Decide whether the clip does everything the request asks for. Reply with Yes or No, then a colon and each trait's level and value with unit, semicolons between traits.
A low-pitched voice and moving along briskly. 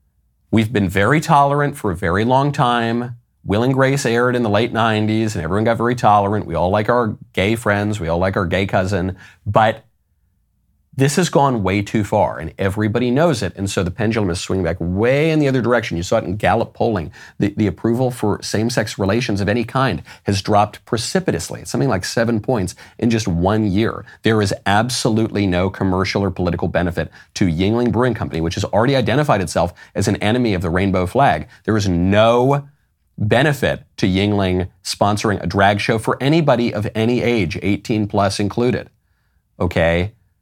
No: low, 105 Hz; average, 185 wpm